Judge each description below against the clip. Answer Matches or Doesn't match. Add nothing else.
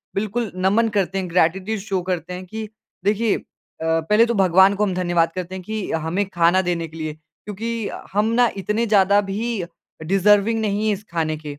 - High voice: Matches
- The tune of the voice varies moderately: Matches